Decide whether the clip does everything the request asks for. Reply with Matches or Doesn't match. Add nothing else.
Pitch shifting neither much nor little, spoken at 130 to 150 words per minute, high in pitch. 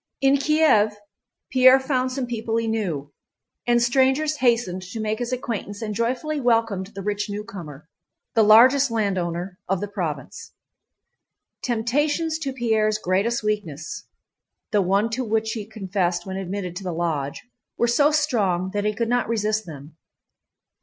Matches